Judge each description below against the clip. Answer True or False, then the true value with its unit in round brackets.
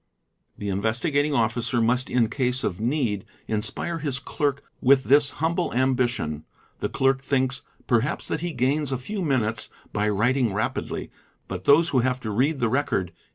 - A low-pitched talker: True (130 Hz)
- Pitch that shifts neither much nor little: True (4.0 semitones)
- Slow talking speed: False (165 wpm)